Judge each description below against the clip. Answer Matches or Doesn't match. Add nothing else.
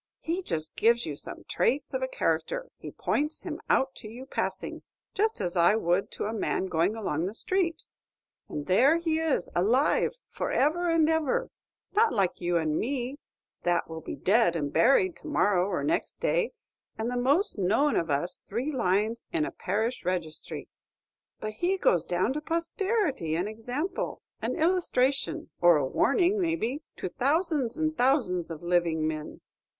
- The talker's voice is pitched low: Doesn't match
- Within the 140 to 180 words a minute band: Matches